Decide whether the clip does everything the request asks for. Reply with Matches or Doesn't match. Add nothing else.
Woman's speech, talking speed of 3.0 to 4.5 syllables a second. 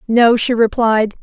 Matches